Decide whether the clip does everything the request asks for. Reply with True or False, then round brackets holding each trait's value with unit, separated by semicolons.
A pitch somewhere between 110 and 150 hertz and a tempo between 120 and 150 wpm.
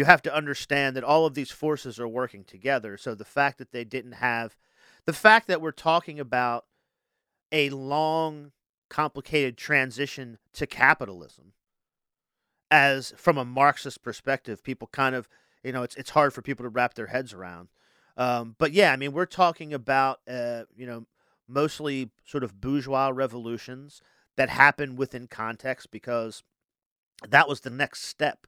False (135 Hz; 160 wpm)